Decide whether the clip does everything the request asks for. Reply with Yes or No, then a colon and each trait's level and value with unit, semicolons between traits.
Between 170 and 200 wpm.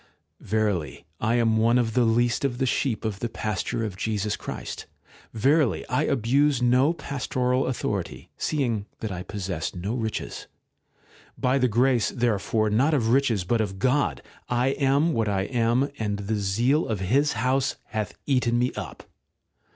No: average, 160 wpm